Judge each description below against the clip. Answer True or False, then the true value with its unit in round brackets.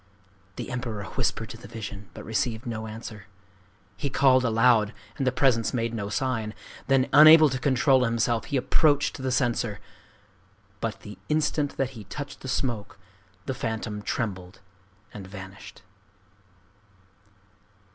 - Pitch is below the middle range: True (115 Hz)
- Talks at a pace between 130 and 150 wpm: True (135 wpm)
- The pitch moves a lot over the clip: False (3.5 semitones)